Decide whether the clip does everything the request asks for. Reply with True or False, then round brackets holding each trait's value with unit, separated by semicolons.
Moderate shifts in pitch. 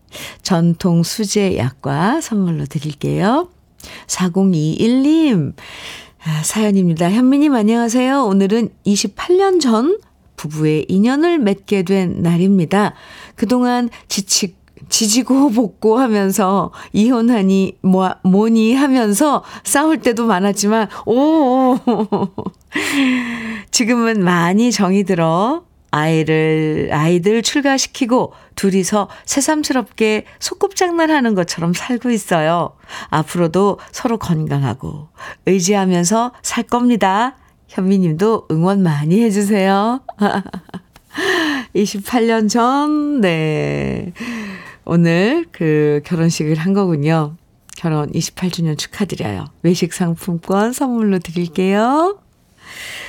False (5.7 semitones)